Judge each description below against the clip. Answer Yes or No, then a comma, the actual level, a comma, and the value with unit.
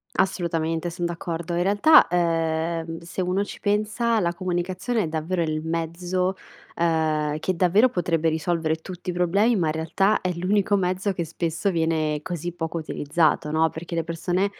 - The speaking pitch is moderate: Yes, medium, 170 Hz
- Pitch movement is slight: Yes, narrow, 2.3 semitones